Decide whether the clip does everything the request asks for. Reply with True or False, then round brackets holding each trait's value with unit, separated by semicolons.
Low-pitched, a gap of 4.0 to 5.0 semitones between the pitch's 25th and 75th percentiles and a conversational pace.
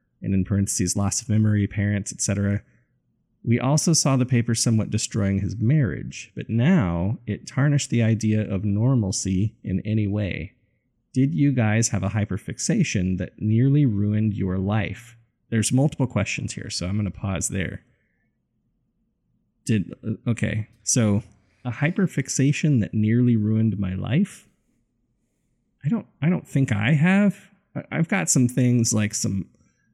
True (110 Hz; 4.3 semitones; 145 wpm)